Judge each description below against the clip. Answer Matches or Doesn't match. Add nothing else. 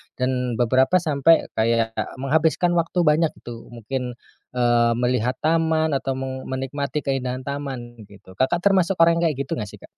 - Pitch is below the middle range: Matches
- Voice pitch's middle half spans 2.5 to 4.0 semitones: Doesn't match